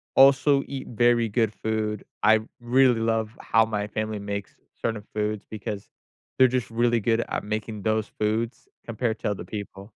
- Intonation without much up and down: Yes, narrow, 2.0 semitones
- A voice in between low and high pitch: No, low, 110 Hz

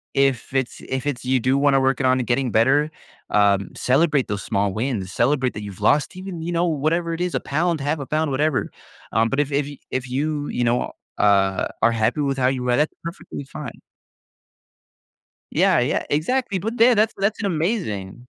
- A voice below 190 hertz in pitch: Yes, low, 135 Hz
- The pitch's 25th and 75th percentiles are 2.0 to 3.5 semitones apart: No, average, 4.5 semitones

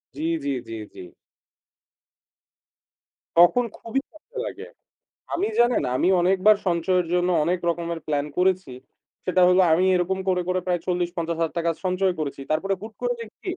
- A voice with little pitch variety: Yes, narrow, 2.2 semitones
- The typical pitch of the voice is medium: Yes, medium, 180 Hz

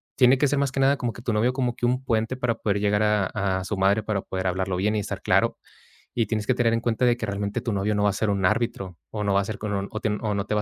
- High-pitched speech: No, low, 105 Hz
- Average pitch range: Yes, average, 3.1 semitones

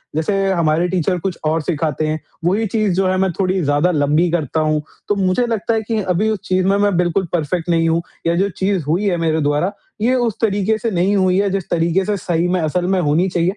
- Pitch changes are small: No, average, 3.1 semitones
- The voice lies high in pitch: No, medium, 180 Hz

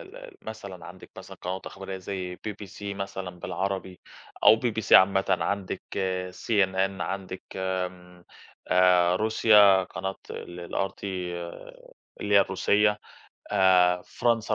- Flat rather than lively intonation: Yes, narrow, 1.9 semitones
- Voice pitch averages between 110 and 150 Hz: No, very low, 95 Hz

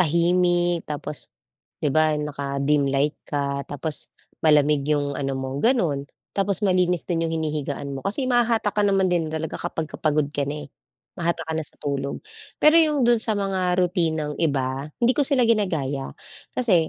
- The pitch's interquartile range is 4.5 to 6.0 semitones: Yes, average, 4.8 semitones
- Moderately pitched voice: Yes, medium, 160 Hz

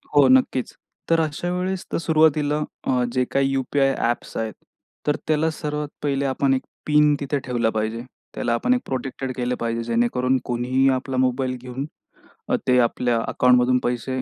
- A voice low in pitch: Yes, low, 130 Hz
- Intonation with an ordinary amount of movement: Yes, average, 3.0 semitones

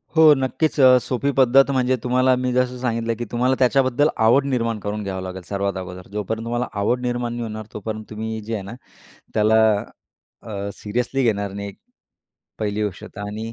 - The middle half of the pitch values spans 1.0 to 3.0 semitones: No, average, 3.4 semitones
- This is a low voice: Yes, low, 115 Hz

